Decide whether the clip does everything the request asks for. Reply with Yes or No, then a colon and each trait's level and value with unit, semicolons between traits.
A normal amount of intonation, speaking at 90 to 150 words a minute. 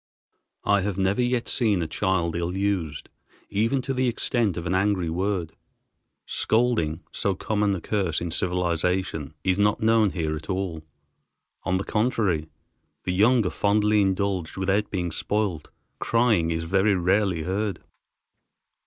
Yes: average, 3.3 semitones; average, 145 wpm